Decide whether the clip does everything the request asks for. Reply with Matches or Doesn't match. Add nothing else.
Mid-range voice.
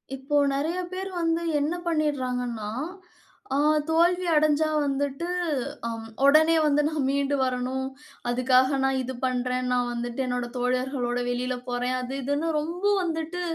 Doesn't match